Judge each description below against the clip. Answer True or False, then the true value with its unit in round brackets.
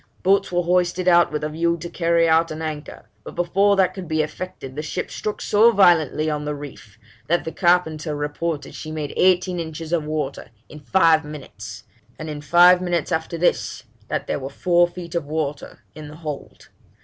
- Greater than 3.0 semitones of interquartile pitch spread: False (2.7 semitones)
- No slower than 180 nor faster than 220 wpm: True (195 wpm)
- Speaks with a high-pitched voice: False (160 Hz)